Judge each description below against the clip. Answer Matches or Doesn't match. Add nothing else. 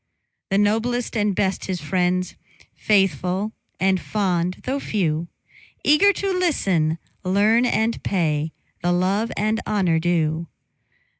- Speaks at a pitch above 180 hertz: Matches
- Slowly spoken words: Matches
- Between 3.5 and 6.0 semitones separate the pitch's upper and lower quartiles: Matches